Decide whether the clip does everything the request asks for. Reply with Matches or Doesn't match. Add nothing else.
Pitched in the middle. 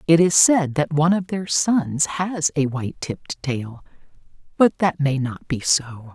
Matches